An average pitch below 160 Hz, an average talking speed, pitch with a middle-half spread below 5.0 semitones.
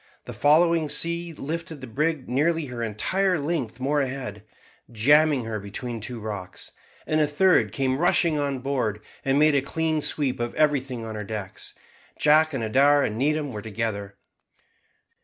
No: low, 135 Hz; average, 160 wpm; average, 5.3 semitones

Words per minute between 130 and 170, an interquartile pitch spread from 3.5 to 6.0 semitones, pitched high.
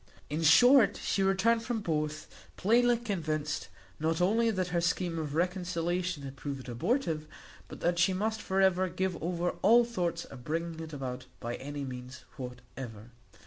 No: average, 160 wpm; average, 4.6 semitones; medium, 170 Hz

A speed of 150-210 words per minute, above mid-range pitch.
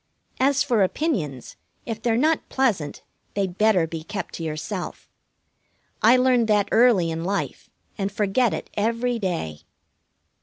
No: average, 140 wpm; high, 210 Hz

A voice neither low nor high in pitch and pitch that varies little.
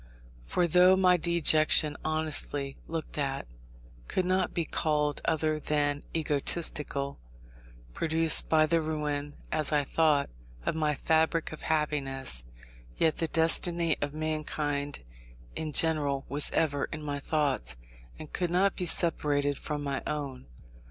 Yes: medium, 155 Hz; narrow, 2.0 semitones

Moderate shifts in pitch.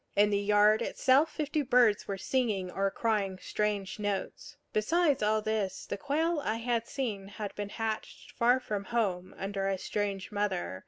Yes: average, 3.3 semitones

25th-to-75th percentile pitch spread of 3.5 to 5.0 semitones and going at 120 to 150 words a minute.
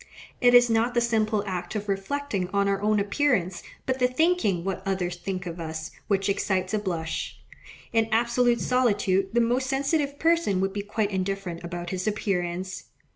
No: average, 4.4 semitones; average, 175 wpm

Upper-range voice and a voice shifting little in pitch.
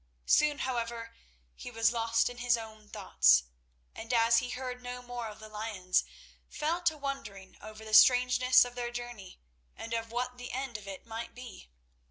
Yes: high, 235 Hz; narrow, 2.3 semitones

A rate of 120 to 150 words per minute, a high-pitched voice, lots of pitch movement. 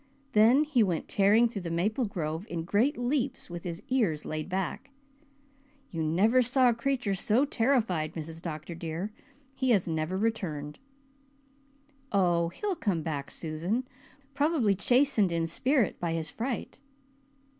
Yes: average, 145 wpm; high, 195 Hz; wide, 6.6 semitones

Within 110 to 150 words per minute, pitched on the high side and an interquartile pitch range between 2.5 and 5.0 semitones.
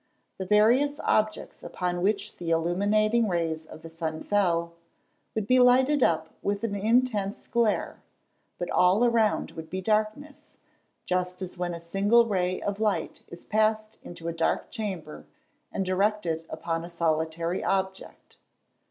Yes: average, 145 wpm; high, 195 Hz; average, 4.2 semitones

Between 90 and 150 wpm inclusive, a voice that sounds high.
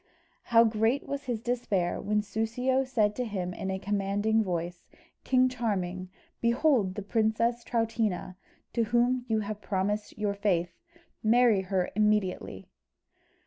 Yes: slow, 135 wpm; high, 215 Hz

